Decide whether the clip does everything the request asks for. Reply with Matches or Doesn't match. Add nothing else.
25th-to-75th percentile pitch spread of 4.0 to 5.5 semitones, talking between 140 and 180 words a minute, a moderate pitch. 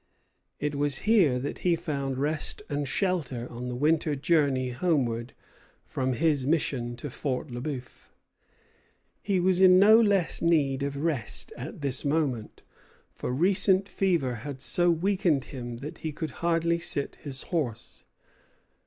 Matches